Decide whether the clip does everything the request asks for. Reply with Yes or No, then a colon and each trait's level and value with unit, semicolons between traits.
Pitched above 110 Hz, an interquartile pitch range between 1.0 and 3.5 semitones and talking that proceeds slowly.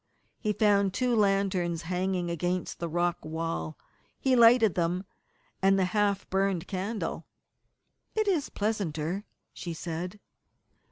Yes: high, 190 Hz; average, 3.2 semitones; slow, 120 wpm